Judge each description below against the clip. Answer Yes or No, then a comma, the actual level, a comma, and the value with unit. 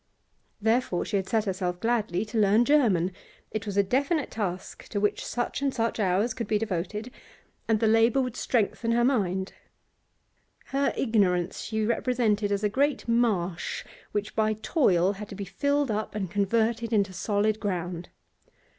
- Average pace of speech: Yes, average, 165 wpm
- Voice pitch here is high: Yes, high, 215 Hz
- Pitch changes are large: No, average, 3.2 semitones